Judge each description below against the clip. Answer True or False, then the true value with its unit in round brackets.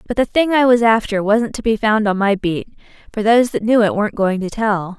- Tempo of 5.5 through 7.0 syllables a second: True (5.6 syllables/s)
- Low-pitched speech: False (215 Hz)